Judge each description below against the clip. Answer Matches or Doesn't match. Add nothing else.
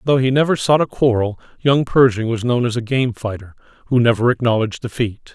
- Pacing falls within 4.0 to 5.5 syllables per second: Doesn't match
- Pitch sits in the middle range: Doesn't match